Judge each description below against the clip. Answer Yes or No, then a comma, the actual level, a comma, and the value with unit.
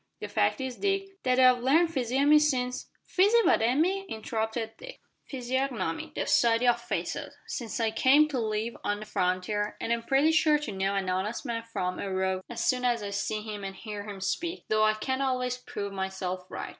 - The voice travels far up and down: No, average, 4.6 semitones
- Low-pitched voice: No, high, 235 Hz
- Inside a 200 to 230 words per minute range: Yes, fast, 205 wpm